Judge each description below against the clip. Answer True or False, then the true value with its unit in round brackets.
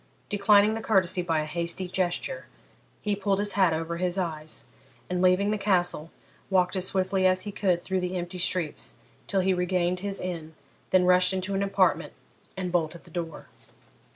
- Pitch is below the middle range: False (185 Hz)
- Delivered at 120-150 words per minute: False (180 wpm)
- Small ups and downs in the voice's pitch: True (1.9 semitones)